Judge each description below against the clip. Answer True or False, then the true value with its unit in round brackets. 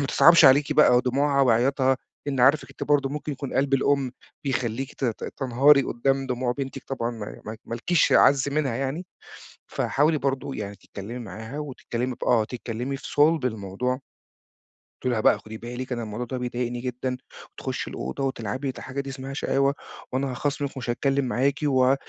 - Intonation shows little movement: True (2.3 semitones)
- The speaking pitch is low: True (130 Hz)